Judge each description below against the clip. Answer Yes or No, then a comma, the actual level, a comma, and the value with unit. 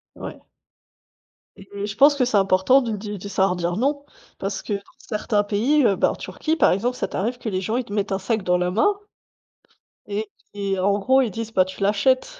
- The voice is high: Yes, high, 205 Hz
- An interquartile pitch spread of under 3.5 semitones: No, average, 3.8 semitones